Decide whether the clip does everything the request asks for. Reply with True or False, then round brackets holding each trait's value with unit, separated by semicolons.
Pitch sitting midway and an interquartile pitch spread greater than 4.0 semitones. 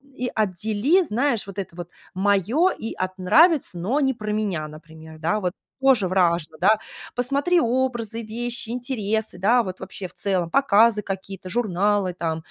False (210 Hz; 4.8 semitones)